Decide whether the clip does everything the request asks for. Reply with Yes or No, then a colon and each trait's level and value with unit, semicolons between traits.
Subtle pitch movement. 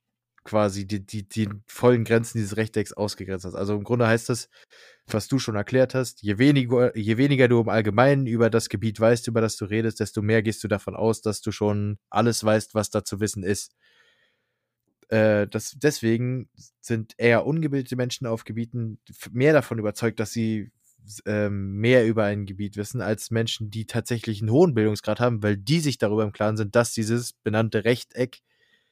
Yes: narrow, 2.2 semitones